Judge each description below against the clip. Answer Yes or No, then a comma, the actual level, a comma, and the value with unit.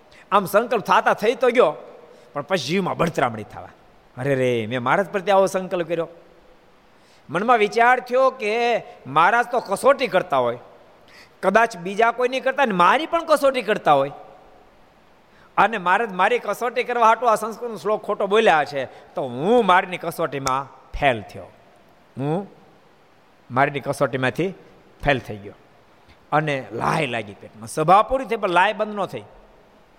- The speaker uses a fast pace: Yes, fast, 150 wpm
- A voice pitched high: Yes, high, 195 Hz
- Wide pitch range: Yes, wide, 8.3 semitones